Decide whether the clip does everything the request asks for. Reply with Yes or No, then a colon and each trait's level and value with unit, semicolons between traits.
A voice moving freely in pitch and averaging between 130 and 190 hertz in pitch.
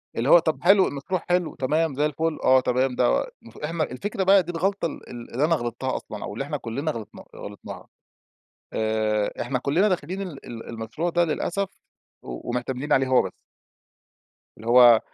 Yes: wide, 5.9 semitones; medium, 140 Hz